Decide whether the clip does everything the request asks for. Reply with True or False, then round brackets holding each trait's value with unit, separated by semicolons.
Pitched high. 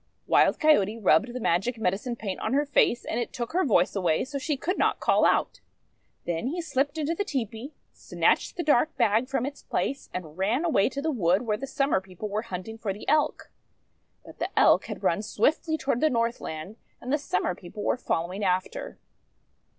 True (235 Hz)